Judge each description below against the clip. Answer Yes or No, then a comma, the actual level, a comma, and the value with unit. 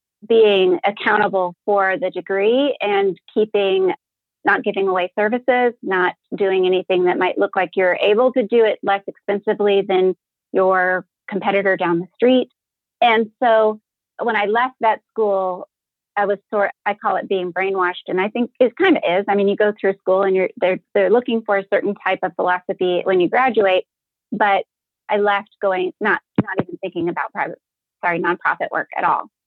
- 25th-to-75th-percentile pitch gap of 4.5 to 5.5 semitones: No, average, 2.7 semitones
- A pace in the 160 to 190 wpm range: Yes, average, 180 wpm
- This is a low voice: No, high, 200 Hz